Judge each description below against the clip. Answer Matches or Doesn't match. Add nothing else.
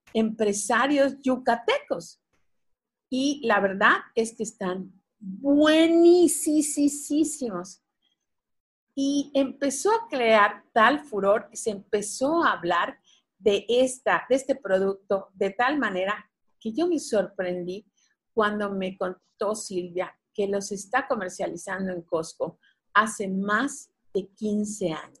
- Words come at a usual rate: Doesn't match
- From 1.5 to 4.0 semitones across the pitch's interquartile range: Doesn't match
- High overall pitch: Matches